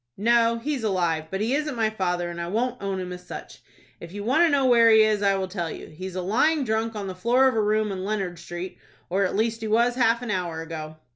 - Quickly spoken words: Yes, fast, 265 wpm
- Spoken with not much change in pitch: No, average, 4.2 semitones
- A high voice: Yes, high, 210 Hz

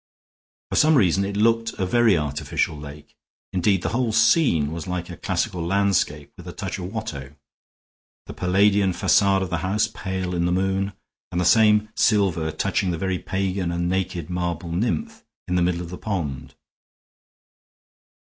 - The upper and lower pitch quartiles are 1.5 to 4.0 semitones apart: Yes, average, 2.8 semitones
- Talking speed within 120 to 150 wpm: No, average, 165 wpm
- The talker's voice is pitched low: Yes, very low, 95 Hz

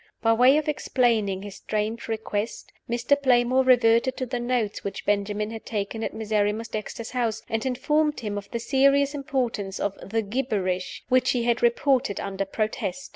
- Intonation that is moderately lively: Yes, average, 3.5 semitones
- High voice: Yes, high, 230 Hz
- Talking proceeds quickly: No, average, 170 wpm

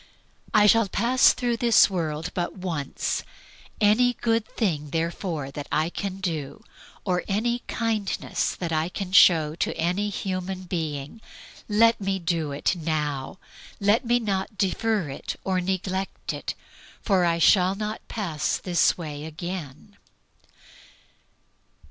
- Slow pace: Yes, slow, 130 wpm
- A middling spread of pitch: Yes, average, 4.5 semitones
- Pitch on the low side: No, medium, 185 Hz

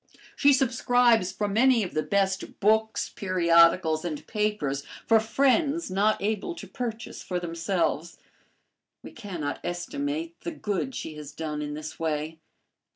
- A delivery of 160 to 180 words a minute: No, average, 140 wpm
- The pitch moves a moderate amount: No, wide, 6.2 semitones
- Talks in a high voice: Yes, high, 195 Hz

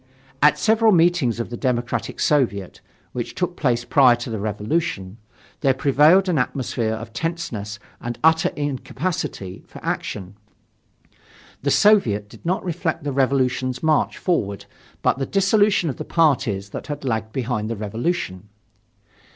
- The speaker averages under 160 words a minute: Yes, average, 145 wpm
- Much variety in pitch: Yes, wide, 6.8 semitones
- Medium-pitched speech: No, low, 130 Hz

